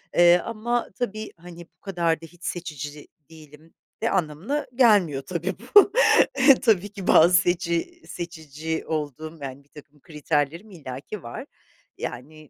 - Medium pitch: Yes, medium, 165 Hz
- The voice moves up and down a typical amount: Yes, average, 4.1 semitones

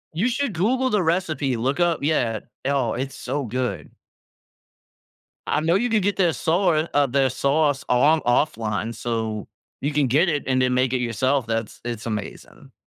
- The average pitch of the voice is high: No, medium, 140 Hz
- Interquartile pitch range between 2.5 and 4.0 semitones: No, average, 5.2 semitones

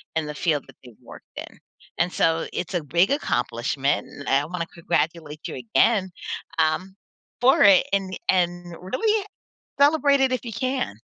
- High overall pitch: No, medium, 175 Hz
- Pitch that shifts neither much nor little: No, wide, 7.0 semitones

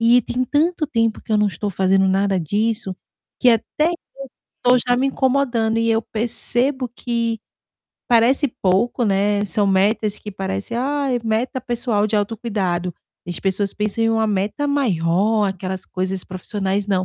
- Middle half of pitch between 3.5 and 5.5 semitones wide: Yes, average, 3.9 semitones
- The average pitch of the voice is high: Yes, high, 220 Hz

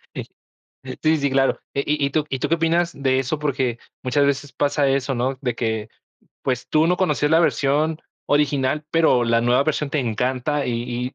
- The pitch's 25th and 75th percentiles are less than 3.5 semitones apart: Yes, average, 2.9 semitones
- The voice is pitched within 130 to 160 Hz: Yes, medium, 140 Hz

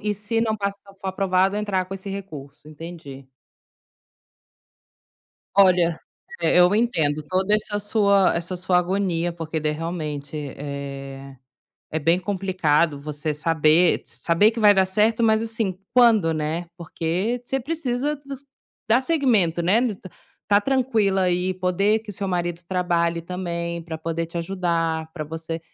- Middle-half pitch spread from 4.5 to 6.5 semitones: No, average, 4.0 semitones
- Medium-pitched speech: Yes, medium, 180 Hz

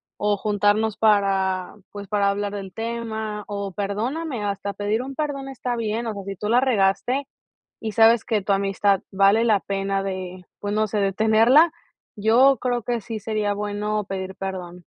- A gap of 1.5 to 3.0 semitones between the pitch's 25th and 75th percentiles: Yes, narrow, 2.4 semitones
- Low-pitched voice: No, high, 210 Hz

